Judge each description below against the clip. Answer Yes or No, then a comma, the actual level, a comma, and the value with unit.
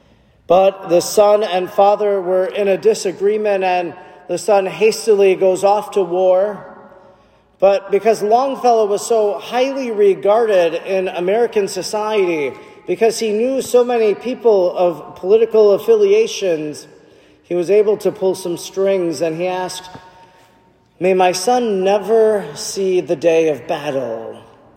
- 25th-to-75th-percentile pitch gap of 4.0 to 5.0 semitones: No, average, 2.9 semitones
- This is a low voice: No, high, 195 Hz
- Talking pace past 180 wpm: No, slow, 135 wpm